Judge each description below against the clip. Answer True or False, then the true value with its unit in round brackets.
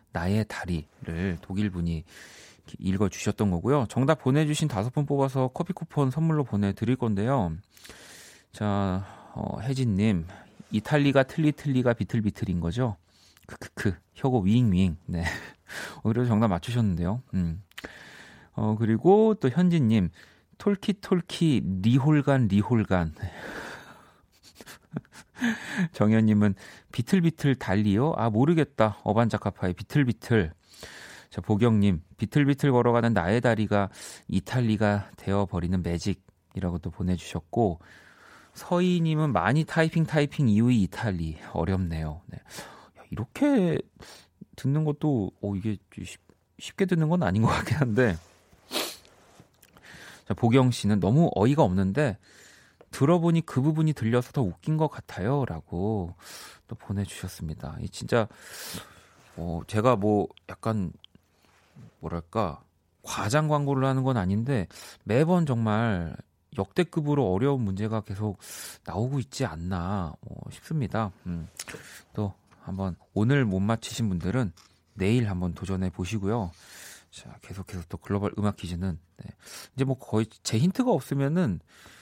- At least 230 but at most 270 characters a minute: True (260 characters per minute)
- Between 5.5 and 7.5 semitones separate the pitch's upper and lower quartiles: True (6.4 semitones)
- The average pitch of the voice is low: True (105 Hz)